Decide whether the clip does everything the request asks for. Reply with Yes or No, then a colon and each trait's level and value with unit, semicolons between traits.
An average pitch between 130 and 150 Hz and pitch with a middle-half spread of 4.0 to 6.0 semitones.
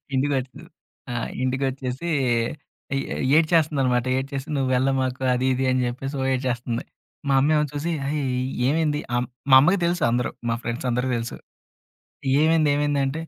No: low, 135 Hz; average, 2.7 semitones